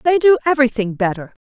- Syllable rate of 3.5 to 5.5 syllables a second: No, 6.8 syllables/s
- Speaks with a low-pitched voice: No, very high, 255 Hz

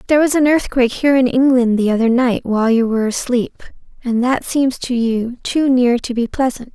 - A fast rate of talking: Yes, fast, 215 wpm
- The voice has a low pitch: No, very high, 250 Hz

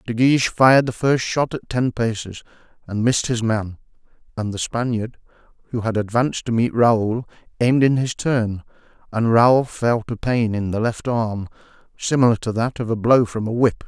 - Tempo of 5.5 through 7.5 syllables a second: No, 5.0 syllables/s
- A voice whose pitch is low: Yes, low, 115 Hz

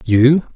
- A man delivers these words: Yes, male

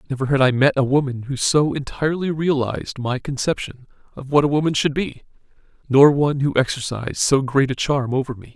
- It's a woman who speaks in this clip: No, male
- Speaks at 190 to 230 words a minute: Yes, average, 195 wpm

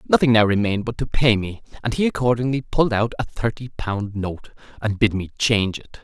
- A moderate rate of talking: No, fast, 210 wpm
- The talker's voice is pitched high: No, low, 110 Hz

